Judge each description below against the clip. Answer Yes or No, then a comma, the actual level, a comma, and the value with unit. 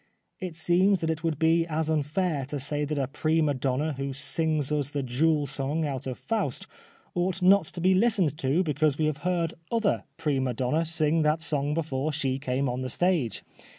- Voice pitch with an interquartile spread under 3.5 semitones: Yes, average, 3.1 semitones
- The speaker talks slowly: No, fast, 205 wpm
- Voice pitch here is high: No, medium, 155 Hz